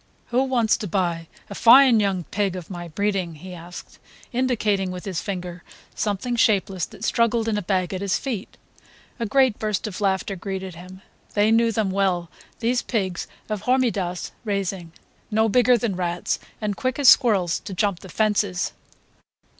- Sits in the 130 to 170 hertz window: No, high, 200 Hz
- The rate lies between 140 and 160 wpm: No, average, 170 wpm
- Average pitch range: Yes, average, 3.6 semitones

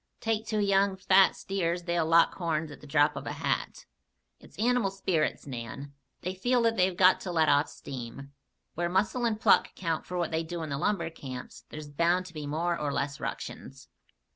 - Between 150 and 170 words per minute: No, average, 200 wpm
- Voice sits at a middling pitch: Yes, medium, 170 Hz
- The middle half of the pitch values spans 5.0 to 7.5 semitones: No, average, 4.2 semitones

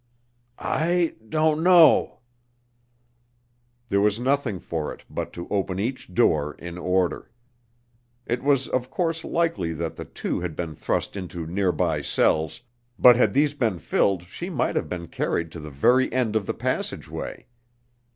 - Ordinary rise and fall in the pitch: No, wide, 7.8 semitones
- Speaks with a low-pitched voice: Yes, low, 100 Hz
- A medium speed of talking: Yes, average, 150 wpm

